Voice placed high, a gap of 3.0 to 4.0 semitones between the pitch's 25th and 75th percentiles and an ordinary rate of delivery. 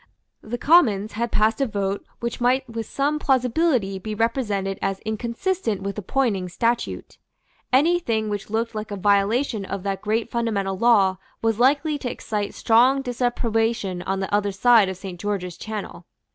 Yes: high, 220 Hz; average, 3.5 semitones; average, 165 wpm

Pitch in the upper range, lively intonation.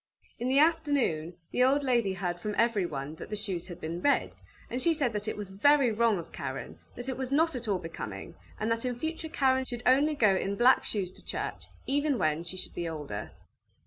Yes: high, 230 Hz; wide, 6.9 semitones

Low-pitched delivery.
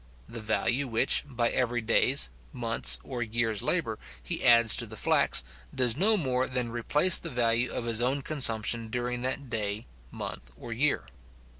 Yes: low, 120 Hz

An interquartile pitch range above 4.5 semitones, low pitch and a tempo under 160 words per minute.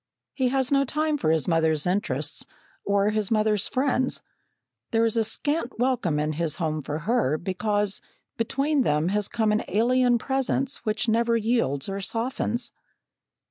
No: wide, 5.6 semitones; high, 220 Hz; average, 150 wpm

